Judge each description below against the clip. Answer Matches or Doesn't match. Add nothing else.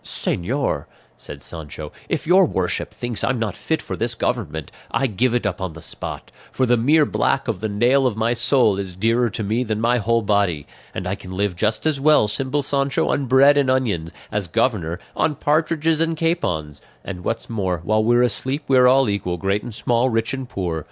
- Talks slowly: Doesn't match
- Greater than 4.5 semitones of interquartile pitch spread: Matches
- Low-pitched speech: Matches